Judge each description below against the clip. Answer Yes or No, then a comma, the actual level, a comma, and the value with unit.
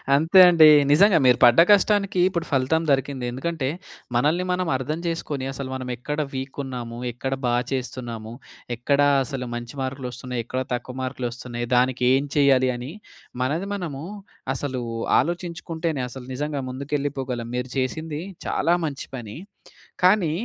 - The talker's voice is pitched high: No, low, 135 Hz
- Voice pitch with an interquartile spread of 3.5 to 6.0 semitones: Yes, average, 3.9 semitones